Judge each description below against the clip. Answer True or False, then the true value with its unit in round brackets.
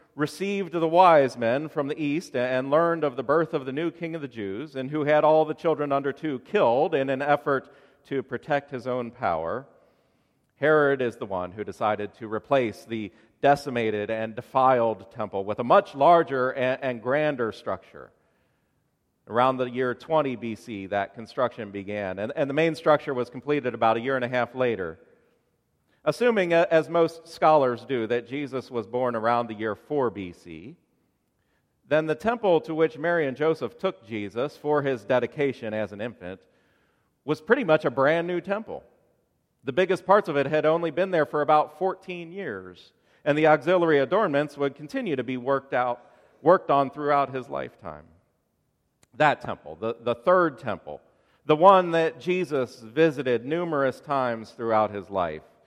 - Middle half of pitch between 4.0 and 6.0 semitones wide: True (4.8 semitones)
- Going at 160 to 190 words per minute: True (170 wpm)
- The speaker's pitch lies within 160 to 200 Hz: False (140 Hz)